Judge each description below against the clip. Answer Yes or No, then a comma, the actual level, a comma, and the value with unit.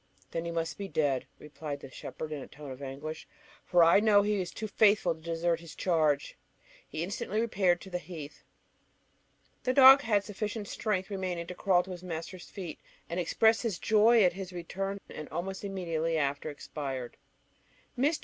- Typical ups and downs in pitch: Yes, average, 4.2 semitones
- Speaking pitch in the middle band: Yes, medium, 175 Hz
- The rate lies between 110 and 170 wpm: No, average, 180 wpm